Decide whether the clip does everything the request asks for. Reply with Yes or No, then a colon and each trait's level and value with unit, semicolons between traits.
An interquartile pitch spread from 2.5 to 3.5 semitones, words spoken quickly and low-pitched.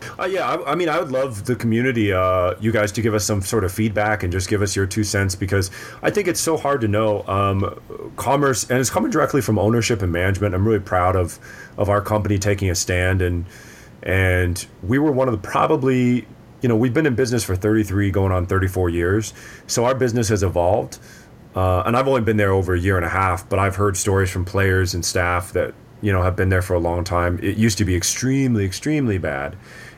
No: average, 3.9 semitones; fast, 250 wpm; low, 105 Hz